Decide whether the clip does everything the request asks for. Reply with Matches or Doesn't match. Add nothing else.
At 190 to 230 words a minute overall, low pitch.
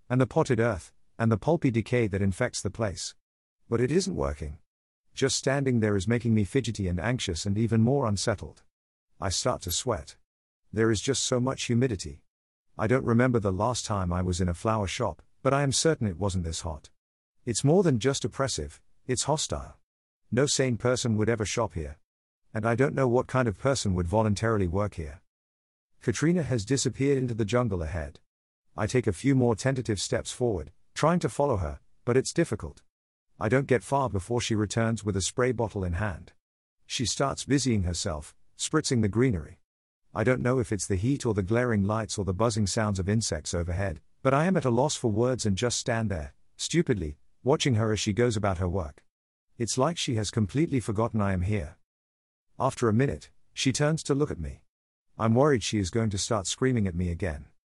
Matches